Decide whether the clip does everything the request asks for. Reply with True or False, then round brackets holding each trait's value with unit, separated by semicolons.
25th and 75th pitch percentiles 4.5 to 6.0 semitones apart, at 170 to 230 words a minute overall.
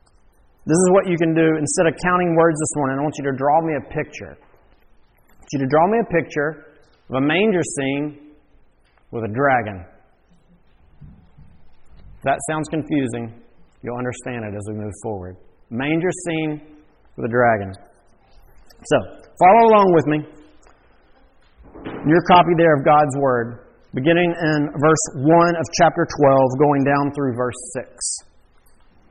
False (4.8 semitones; 155 wpm)